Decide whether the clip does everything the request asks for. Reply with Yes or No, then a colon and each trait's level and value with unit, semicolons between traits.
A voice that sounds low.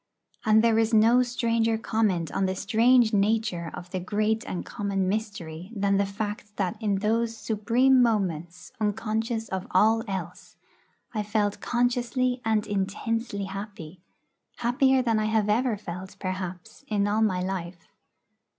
No: high, 210 Hz